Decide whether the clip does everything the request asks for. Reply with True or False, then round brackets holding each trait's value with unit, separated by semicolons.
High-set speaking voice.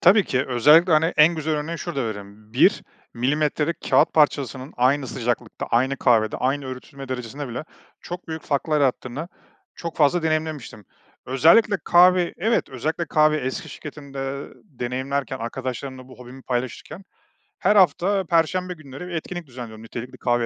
False (140 Hz)